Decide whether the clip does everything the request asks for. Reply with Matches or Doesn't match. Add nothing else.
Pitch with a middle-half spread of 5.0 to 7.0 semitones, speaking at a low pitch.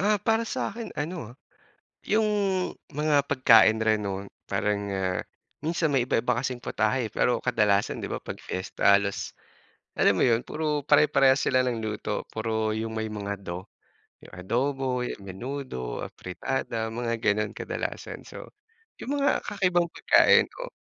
Matches